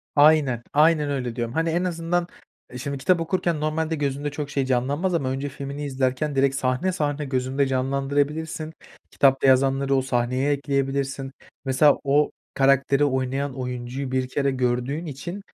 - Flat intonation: Yes, narrow, 2.3 semitones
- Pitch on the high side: No, medium, 140 Hz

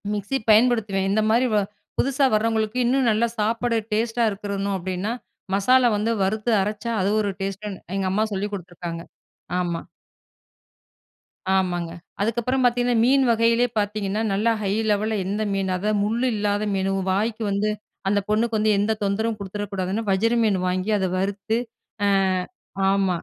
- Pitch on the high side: Yes, high, 210 Hz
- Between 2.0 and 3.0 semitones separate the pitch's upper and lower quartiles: Yes, average, 2.7 semitones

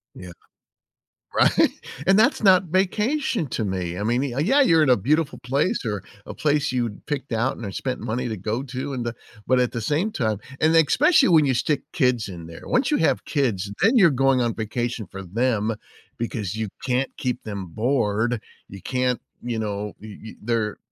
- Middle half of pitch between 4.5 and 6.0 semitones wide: Yes, wide, 5.4 semitones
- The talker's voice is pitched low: Yes, low, 125 Hz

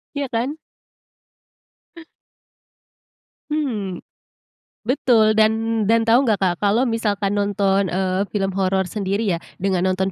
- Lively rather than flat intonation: No, average, 2.9 semitones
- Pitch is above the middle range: Yes, high, 205 Hz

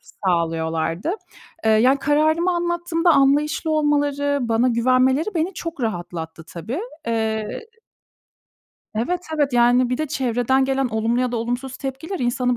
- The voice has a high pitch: Yes, very high, 255 Hz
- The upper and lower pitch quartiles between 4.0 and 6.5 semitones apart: Yes, average, 4.8 semitones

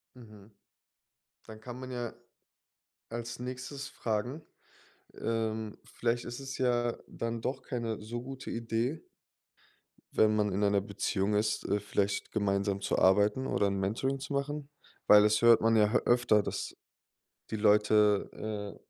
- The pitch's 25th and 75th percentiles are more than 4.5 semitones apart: No, average, 2.9 semitones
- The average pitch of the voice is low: Yes, low, 110 Hz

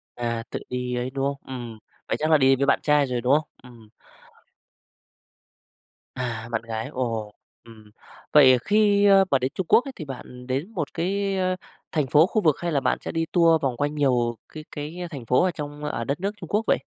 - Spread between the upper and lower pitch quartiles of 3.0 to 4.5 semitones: No, average, 4.9 semitones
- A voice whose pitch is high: No, medium, 140 Hz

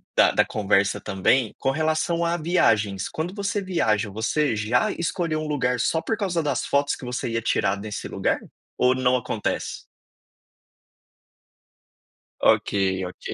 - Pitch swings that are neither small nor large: No, wide, 7.4 semitones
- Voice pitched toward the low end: Yes, low, 130 Hz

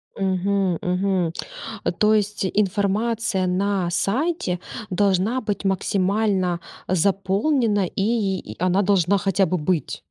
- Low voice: No, high, 195 Hz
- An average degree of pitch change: No, narrow, 2.1 semitones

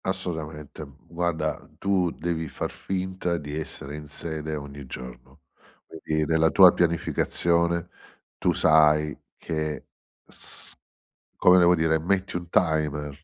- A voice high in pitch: No, very low, 80 Hz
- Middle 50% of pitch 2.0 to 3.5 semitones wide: Yes, narrow, 2.3 semitones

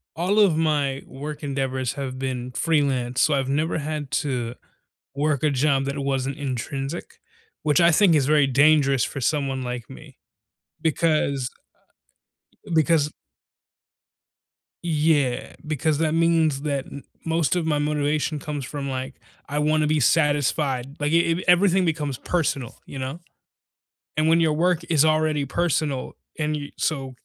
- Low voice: No, medium, 145 Hz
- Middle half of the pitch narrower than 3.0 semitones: Yes, narrow, 2.6 semitones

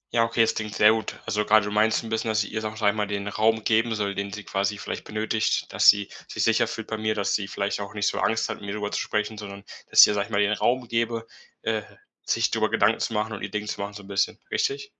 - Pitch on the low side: Yes, low, 105 Hz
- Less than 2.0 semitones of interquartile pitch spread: Yes, narrow, 1.5 semitones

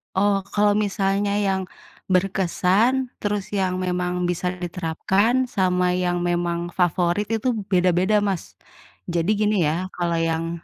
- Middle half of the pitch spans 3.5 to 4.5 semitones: No, narrow, 2.6 semitones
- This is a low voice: No, medium, 185 Hz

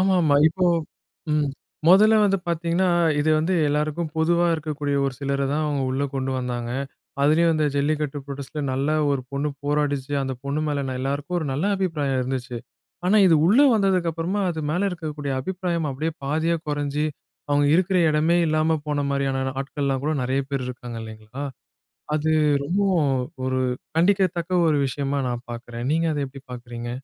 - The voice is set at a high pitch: No, medium, 150 Hz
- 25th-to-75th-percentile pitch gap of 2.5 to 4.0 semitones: Yes, average, 3.5 semitones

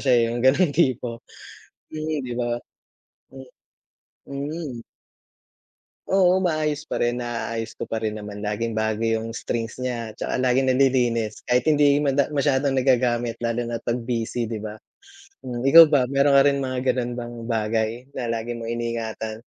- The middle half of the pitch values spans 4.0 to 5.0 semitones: No, average, 3.1 semitones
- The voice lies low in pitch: Yes, low, 120 Hz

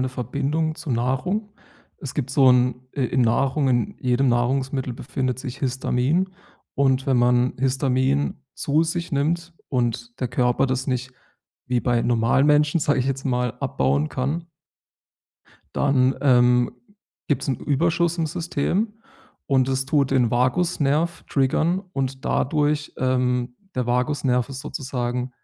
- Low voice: Yes, low, 130 Hz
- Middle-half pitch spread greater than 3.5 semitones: No, average, 2.8 semitones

